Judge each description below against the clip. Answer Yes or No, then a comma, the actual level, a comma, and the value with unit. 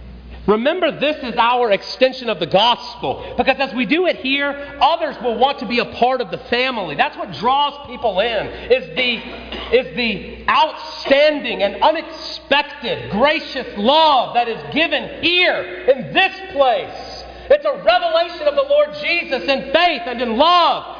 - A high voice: Yes, very high, 280 Hz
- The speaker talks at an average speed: Yes, average, 165 wpm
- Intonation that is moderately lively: Yes, average, 4.5 semitones